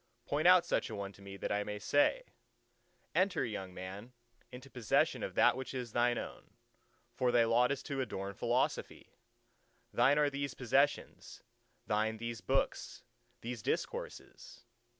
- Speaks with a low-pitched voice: Yes, low, 120 Hz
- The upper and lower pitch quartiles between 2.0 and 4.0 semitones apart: No, average, 4.7 semitones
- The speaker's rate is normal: Yes, average, 150 wpm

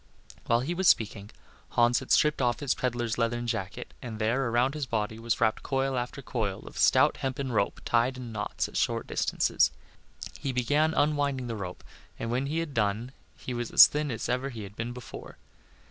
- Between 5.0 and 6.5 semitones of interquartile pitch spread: No, average, 2.9 semitones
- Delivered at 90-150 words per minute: No, average, 195 wpm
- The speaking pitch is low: Yes, low, 120 Hz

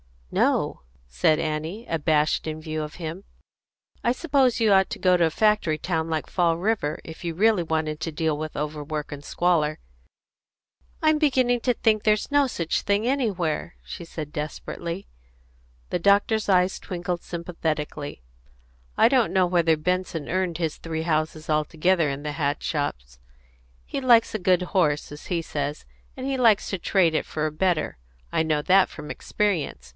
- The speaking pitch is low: No, medium, 170 Hz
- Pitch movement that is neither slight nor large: Yes, average, 4.5 semitones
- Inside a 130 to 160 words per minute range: No, average, 170 wpm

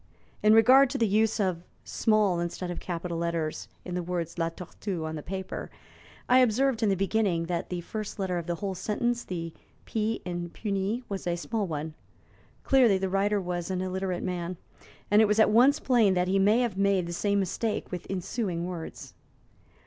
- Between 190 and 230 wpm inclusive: Yes, average, 195 wpm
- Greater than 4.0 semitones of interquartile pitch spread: No, average, 3.6 semitones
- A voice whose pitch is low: No, high, 190 Hz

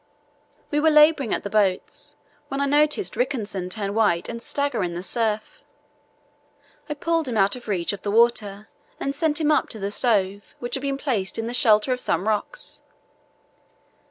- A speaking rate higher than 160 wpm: Yes, average, 185 wpm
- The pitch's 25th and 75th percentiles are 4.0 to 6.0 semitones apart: Yes, wide, 5.6 semitones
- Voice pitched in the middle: No, high, 230 Hz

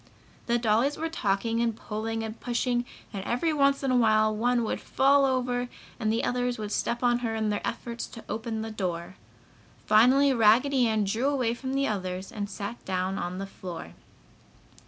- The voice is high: Yes, high, 230 Hz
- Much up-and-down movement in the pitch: No, average, 2.8 semitones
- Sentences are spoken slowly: No, average, 185 wpm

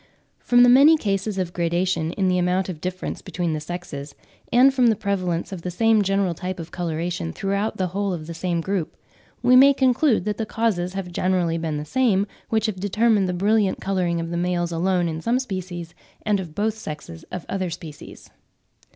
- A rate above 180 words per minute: Yes, average, 200 wpm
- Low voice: No, medium, 185 Hz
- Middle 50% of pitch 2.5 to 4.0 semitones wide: Yes, average, 3.5 semitones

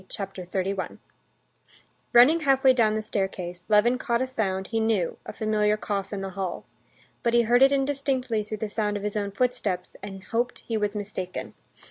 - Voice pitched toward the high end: Yes, high, 215 Hz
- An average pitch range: Yes, average, 3.6 semitones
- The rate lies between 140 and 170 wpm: No, average, 180 wpm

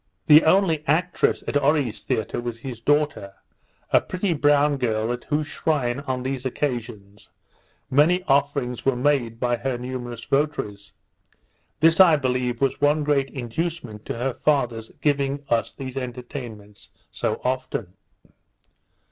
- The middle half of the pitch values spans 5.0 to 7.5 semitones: No, average, 3.5 semitones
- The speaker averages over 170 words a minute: No, slow, 135 wpm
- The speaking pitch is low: Yes, low, 130 Hz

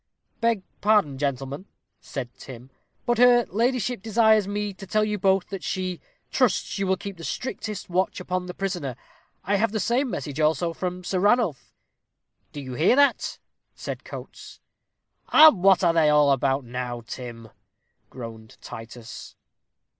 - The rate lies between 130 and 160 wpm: Yes, average, 155 wpm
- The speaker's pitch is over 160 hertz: Yes, medium, 185 Hz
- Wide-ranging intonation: Yes, wide, 7.4 semitones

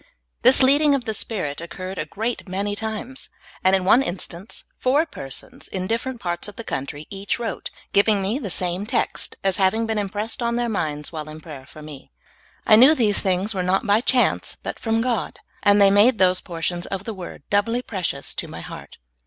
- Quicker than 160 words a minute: Yes, average, 200 wpm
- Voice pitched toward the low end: No, high, 200 Hz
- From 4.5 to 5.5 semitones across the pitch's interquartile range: No, average, 4.0 semitones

